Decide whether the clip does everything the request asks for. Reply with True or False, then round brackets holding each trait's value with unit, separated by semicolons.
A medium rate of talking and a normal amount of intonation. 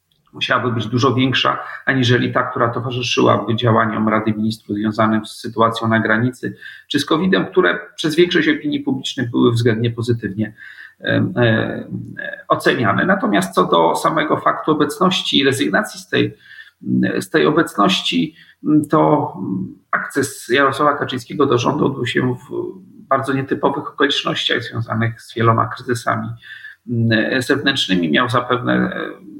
True (125 wpm; 3.5 semitones)